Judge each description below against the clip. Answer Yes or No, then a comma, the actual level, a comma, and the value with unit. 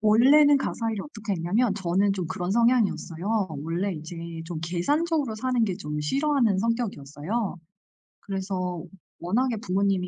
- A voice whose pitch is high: Yes, high, 200 Hz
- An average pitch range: Yes, average, 4.9 semitones